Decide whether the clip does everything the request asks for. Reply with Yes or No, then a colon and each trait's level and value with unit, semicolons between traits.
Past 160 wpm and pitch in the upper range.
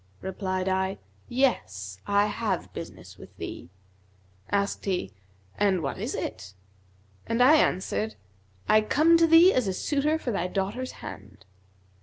No: average, 140 wpm; high, 200 Hz